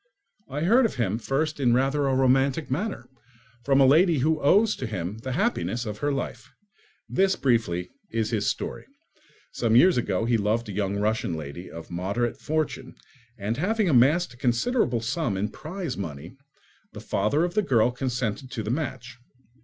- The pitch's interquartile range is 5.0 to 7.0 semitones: Yes, wide, 5.4 semitones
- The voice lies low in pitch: Yes, low, 125 Hz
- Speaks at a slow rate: No, average, 175 wpm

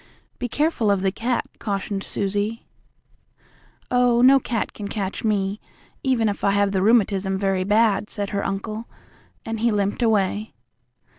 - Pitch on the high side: Yes, high, 210 Hz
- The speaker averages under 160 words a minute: Yes, average, 150 wpm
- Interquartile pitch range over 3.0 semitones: No, narrow, 2.6 semitones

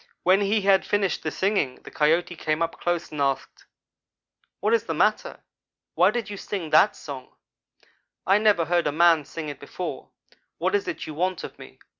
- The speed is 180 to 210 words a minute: Yes, average, 190 wpm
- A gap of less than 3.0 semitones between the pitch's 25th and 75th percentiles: No, average, 4.5 semitones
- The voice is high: No, medium, 175 Hz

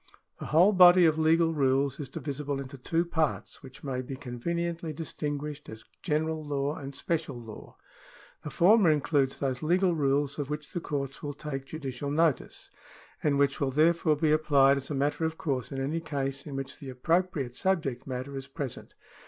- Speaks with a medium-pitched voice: Yes, medium, 145 Hz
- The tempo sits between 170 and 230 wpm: Yes, average, 180 wpm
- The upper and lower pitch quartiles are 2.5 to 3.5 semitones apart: Yes, average, 2.8 semitones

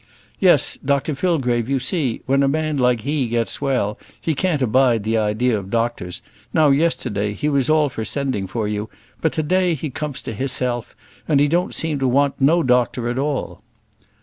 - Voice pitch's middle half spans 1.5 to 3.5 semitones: No, average, 4.2 semitones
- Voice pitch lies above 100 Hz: Yes, low, 135 Hz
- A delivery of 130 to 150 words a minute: No, average, 185 wpm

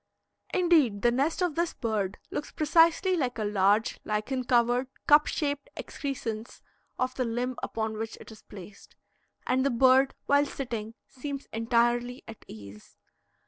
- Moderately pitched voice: No, high, 245 Hz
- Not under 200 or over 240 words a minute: No, average, 145 wpm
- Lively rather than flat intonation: No, average, 4.3 semitones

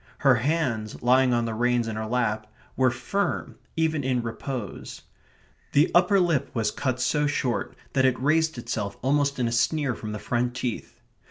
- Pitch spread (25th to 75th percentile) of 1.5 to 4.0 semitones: Yes, average, 3.7 semitones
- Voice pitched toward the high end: No, low, 125 Hz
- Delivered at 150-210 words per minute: Yes, average, 175 wpm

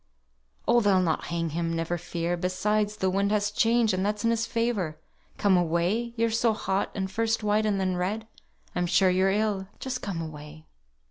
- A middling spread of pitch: Yes, average, 3.7 semitones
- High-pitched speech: Yes, high, 195 Hz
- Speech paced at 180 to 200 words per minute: Yes, average, 190 wpm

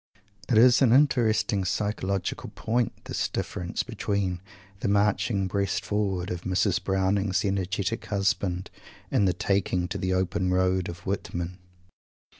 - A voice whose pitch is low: Yes, very low, 95 Hz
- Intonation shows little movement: Yes, narrow, 1.9 semitones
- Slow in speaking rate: Yes, slow, 130 wpm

